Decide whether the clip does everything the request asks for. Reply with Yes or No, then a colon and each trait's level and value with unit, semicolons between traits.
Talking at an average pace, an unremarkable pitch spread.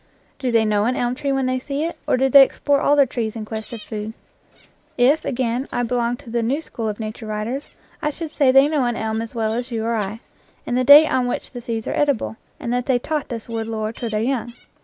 No: fast, 260 wpm; average, 3.2 semitones